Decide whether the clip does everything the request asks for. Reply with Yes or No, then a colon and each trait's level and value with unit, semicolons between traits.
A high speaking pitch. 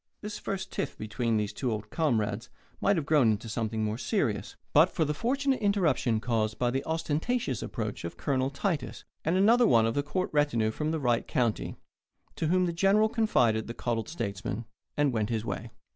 No: low, 130 Hz